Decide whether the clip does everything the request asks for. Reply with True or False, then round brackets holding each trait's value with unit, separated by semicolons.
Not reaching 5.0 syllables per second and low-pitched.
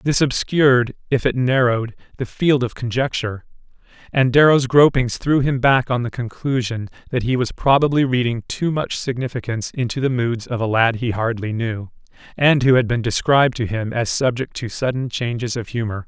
False (5.3 syllables/s; 125 Hz)